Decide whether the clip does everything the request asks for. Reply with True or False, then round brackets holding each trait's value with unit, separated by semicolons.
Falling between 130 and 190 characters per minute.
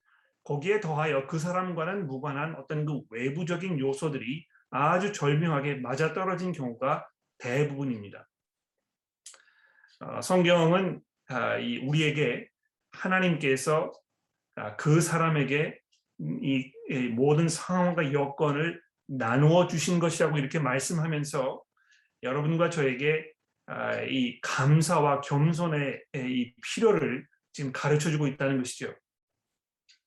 False (235 characters per minute)